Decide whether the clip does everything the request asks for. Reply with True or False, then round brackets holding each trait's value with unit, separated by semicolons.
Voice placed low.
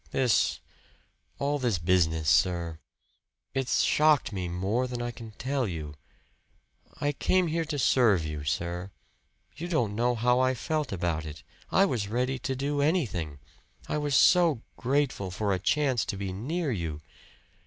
True (120 Hz)